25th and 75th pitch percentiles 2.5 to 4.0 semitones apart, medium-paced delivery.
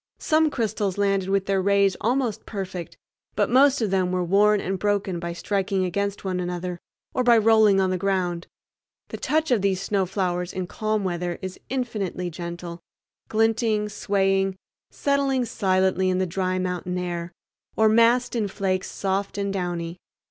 Yes: average, 2.8 semitones; average, 160 wpm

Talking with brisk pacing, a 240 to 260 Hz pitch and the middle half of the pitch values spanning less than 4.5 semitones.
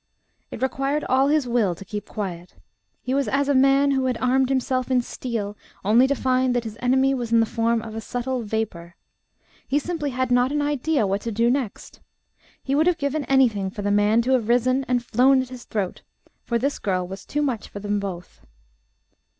Yes: fast, 210 wpm; very high, 250 Hz; average, 3.8 semitones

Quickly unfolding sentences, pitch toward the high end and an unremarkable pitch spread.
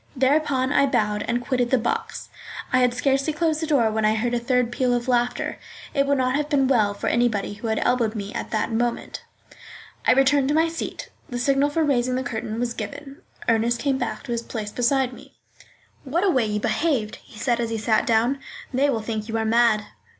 Yes: fast, 220 wpm; high, 245 Hz; average, 3.4 semitones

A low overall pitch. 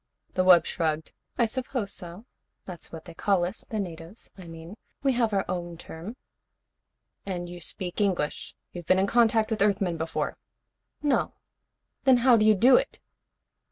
No: high, 190 Hz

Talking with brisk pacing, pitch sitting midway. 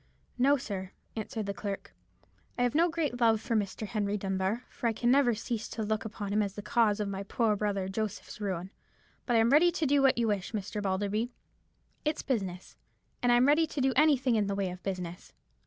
No: fast, 215 wpm; high, 215 Hz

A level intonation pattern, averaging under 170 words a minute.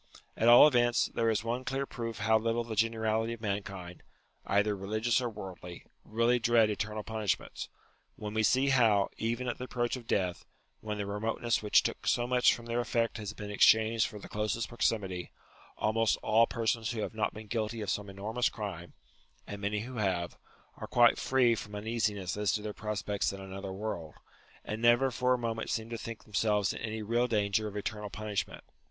No: narrow, 2.2 semitones; average, 195 wpm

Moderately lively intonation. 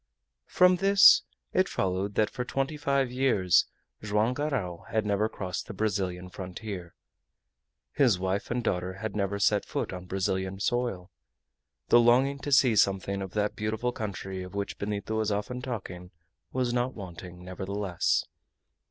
Yes: average, 4.6 semitones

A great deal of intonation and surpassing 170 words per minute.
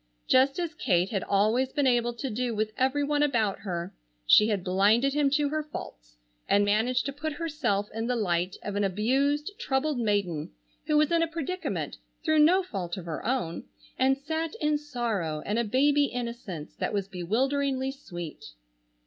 Yes: wide, 6.2 semitones; average, 180 wpm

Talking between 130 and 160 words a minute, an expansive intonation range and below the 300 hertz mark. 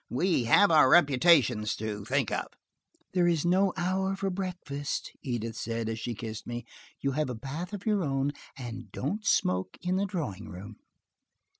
No: average, 170 wpm; wide, 7.9 semitones; medium, 140 Hz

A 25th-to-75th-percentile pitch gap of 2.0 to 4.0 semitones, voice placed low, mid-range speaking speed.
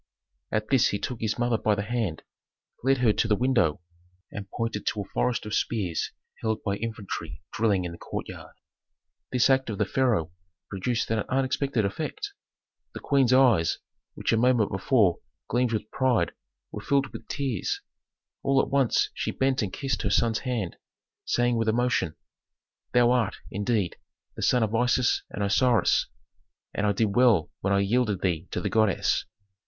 Yes: average, 3.7 semitones; low, 115 Hz; average, 170 wpm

